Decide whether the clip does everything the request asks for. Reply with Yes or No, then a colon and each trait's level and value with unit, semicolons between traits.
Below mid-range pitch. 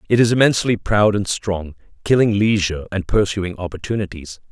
Yes: low, 100 Hz